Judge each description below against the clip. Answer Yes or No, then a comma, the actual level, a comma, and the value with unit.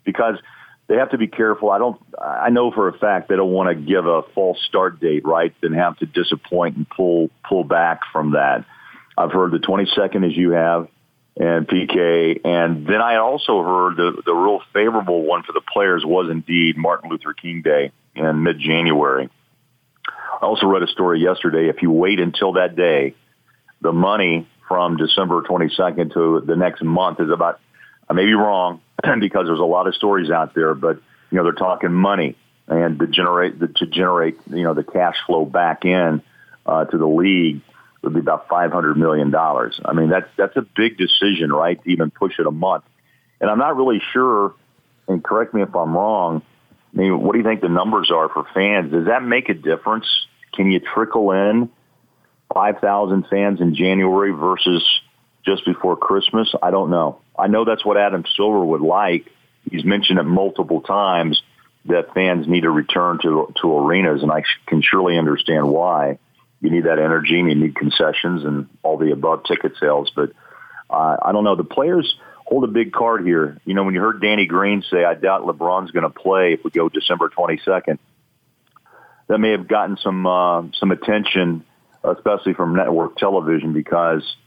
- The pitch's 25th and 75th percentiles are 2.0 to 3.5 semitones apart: Yes, average, 3.2 semitones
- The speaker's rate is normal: Yes, average, 195 wpm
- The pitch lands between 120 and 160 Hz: No, very low, 90 Hz